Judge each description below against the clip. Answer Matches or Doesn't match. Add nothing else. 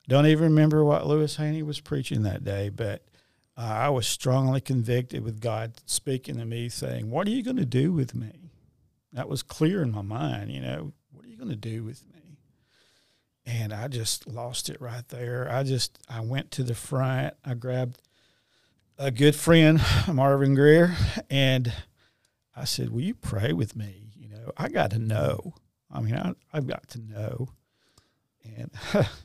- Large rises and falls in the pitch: Doesn't match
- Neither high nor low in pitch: Doesn't match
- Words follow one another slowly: Doesn't match